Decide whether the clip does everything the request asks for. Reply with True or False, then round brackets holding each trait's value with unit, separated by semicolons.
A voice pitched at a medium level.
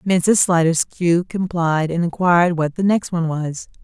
True (170 Hz)